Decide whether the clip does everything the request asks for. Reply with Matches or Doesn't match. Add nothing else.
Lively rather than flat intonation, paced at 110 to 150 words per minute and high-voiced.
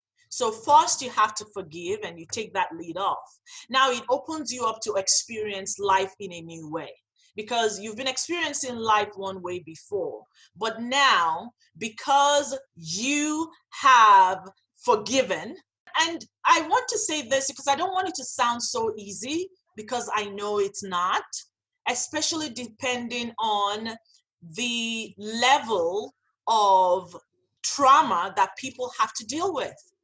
Matches